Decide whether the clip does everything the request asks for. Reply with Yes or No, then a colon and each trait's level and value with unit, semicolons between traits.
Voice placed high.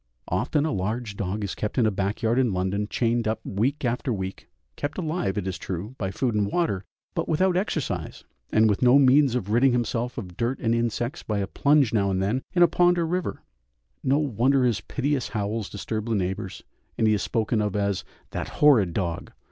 No: low, 115 Hz